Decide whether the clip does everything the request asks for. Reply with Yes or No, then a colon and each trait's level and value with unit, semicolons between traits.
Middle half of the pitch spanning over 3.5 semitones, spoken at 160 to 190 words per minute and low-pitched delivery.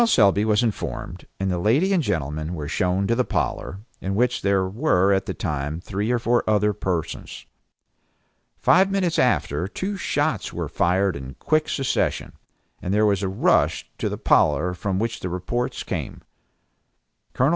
Yes: average, 5.1 semitones; average, 165 wpm; low, 100 Hz